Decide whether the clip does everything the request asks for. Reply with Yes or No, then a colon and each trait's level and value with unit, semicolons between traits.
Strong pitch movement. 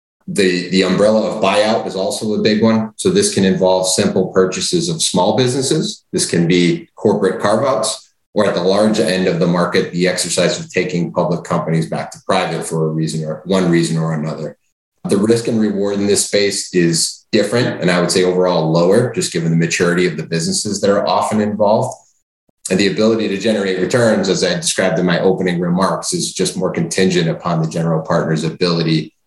No: average, 3.8 semitones